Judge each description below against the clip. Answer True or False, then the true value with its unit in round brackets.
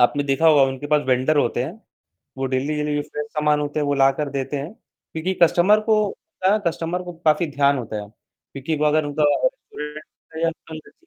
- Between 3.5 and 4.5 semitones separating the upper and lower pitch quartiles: False (2.5 semitones)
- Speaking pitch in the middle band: True (150 Hz)